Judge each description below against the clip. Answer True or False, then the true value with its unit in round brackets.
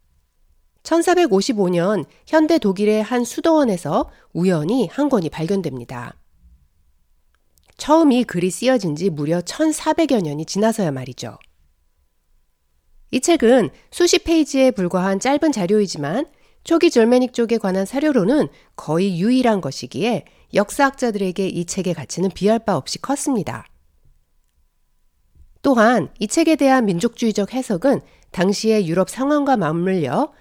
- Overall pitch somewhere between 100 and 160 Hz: False (200 Hz)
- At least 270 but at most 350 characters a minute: False (260 characters per minute)